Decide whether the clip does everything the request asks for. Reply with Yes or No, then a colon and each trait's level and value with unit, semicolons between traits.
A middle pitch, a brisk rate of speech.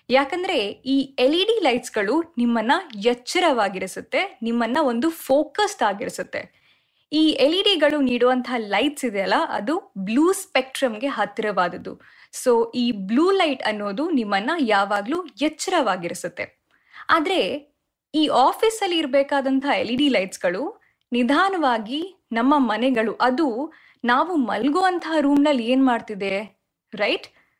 No: very high, 270 Hz; fast, 115 wpm